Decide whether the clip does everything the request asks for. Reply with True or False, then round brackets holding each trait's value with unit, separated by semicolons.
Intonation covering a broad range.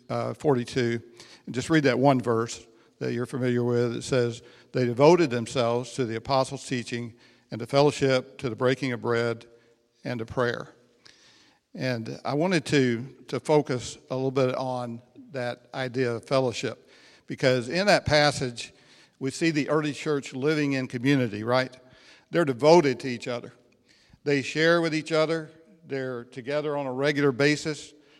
False (3.1 semitones)